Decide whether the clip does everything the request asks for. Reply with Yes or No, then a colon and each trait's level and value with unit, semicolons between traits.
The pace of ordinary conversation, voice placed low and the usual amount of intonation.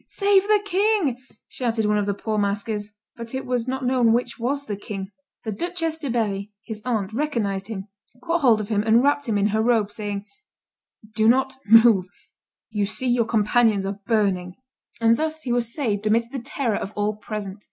No: average, 195 wpm; high, 225 Hz; average, 3.9 semitones